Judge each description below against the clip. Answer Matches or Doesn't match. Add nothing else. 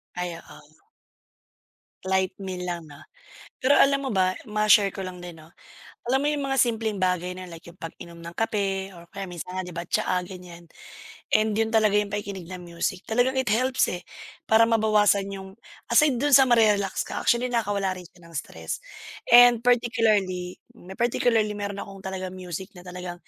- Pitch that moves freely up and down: Doesn't match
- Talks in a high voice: Matches